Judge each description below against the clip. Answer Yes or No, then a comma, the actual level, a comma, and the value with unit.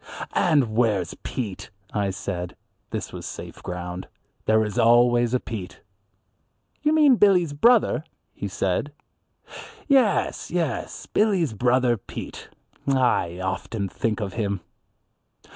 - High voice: No, low, 115 Hz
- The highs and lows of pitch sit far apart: Yes, wide, 7.3 semitones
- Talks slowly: Yes, slow, 115 wpm